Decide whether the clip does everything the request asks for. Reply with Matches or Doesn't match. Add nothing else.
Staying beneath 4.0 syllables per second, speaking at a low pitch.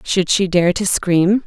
Doesn't match